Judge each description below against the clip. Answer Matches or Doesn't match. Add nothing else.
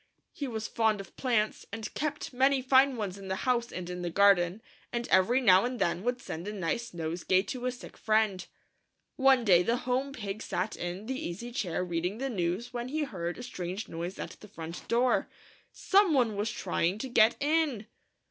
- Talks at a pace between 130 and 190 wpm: Doesn't match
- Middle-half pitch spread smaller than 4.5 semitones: Doesn't match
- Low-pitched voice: Doesn't match